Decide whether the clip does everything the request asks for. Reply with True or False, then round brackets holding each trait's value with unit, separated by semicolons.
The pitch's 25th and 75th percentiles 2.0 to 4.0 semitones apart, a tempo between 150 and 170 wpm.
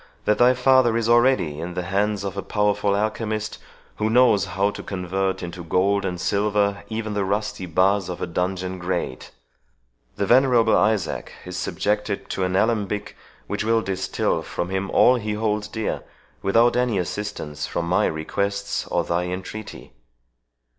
True (2.8 semitones; 160 wpm)